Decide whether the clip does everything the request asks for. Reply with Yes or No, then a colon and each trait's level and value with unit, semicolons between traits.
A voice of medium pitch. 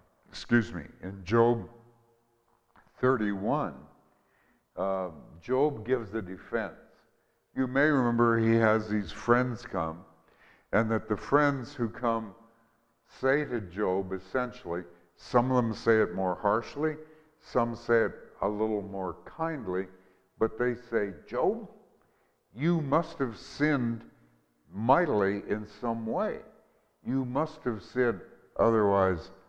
No: low, 115 Hz